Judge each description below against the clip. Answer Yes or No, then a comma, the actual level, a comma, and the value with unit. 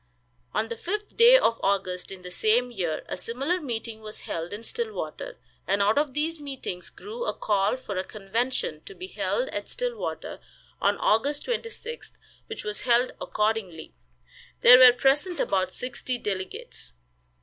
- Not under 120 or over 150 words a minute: No, average, 160 wpm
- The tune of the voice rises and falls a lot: Yes, wide, 8.9 semitones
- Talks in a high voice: Yes, high, 240 Hz